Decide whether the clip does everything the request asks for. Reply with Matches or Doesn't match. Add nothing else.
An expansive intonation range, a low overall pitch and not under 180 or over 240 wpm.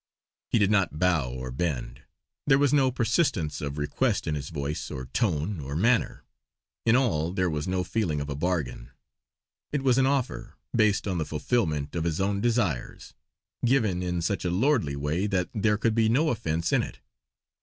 Matches